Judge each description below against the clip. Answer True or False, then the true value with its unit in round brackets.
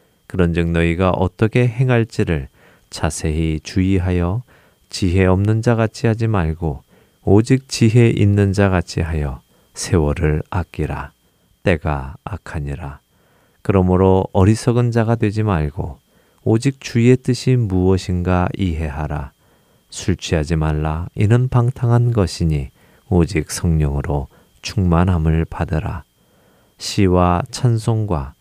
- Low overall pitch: True (90 Hz)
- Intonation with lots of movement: True (5.7 semitones)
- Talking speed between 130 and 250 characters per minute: True (245 characters per minute)